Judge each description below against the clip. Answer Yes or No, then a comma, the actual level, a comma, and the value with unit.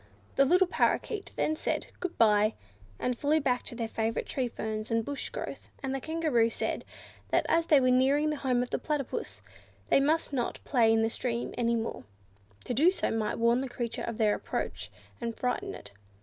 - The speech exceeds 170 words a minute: Yes, average, 200 wpm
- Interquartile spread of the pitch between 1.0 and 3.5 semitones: No, average, 4.0 semitones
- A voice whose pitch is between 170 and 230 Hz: No, very high, 250 Hz